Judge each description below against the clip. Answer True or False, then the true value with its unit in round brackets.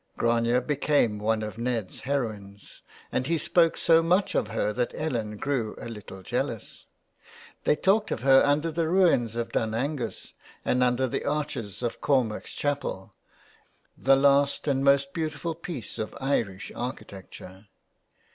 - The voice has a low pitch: True (130 Hz)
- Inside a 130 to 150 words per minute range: True (145 wpm)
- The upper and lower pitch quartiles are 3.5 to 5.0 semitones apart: True (4.7 semitones)